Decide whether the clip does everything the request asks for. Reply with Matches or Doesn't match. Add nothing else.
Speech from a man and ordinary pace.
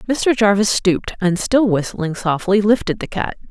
Doesn't match